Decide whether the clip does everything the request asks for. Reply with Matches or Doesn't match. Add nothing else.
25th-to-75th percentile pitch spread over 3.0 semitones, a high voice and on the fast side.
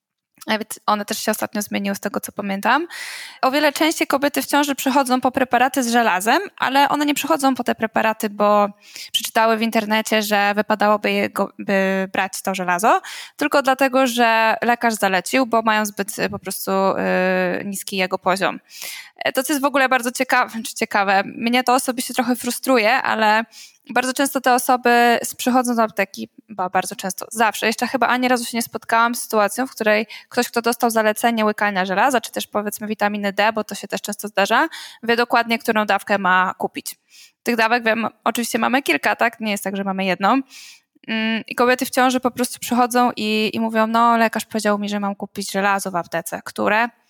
Matches